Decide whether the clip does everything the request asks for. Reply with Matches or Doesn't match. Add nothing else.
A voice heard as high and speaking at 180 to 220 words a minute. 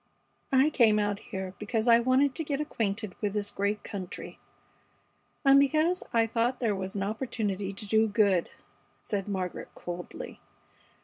Doesn't match